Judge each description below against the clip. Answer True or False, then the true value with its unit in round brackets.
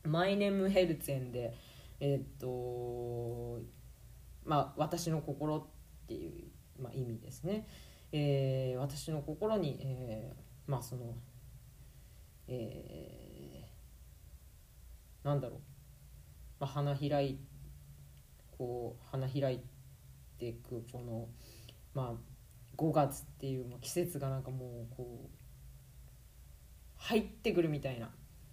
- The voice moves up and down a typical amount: True (3.3 semitones)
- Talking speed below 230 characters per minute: True (200 characters per minute)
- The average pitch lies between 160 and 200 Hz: False (130 Hz)